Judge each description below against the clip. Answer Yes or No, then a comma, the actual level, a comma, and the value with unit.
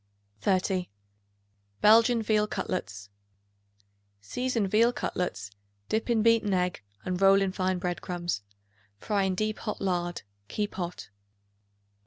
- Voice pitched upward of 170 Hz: Yes, high, 190 Hz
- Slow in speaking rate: Yes, slow, 120 wpm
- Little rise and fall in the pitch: No, average, 3.2 semitones